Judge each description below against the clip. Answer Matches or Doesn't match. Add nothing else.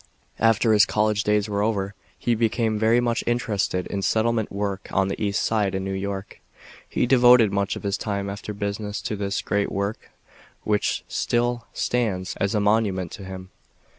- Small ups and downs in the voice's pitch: Matches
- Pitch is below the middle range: Matches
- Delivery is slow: Doesn't match